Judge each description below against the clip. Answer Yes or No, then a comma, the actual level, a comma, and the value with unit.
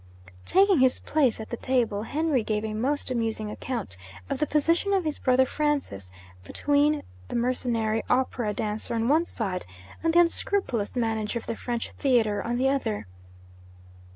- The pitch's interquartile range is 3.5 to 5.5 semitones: Yes, average, 5.0 semitones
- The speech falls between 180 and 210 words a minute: No, average, 160 wpm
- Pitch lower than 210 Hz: No, high, 245 Hz